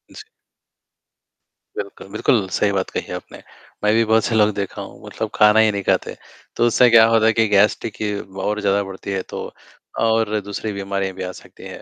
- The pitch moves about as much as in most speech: No, narrow, 2.2 semitones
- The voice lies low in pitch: Yes, low, 105 Hz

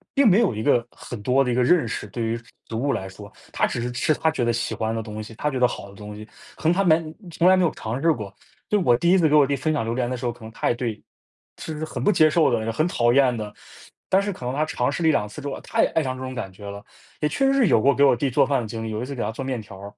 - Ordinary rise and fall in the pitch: No, wide, 5.7 semitones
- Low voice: Yes, low, 125 Hz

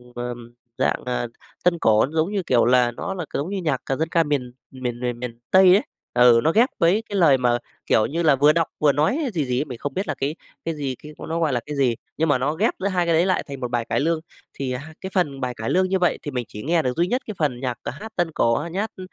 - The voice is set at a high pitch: No, medium, 150 Hz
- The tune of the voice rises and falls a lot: Yes, wide, 5.7 semitones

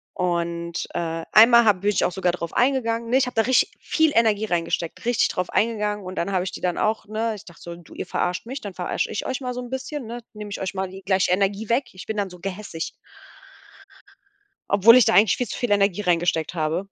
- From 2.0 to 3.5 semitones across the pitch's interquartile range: No, average, 4.3 semitones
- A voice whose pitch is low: No, high, 200 Hz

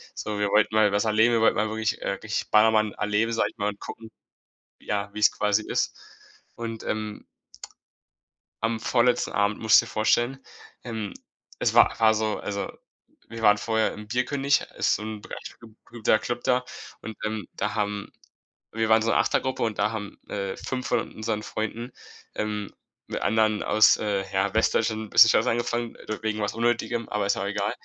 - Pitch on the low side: Yes, low, 110 Hz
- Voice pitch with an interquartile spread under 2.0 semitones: Yes, narrow, 1.5 semitones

